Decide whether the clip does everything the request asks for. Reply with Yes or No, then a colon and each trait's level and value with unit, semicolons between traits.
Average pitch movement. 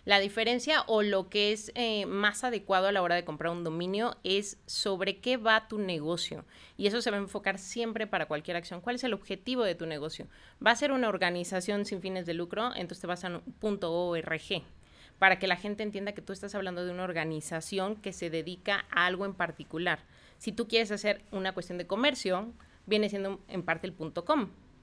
Yes: average, 3.3 semitones